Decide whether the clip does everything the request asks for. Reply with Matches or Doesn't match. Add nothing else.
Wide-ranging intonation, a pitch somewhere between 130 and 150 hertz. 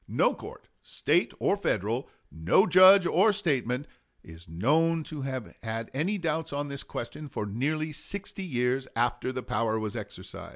Matches